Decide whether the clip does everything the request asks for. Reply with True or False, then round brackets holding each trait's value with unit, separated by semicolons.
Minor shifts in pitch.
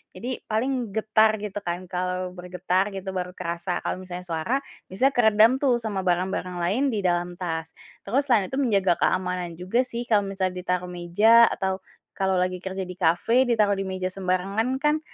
False (3.3 semitones)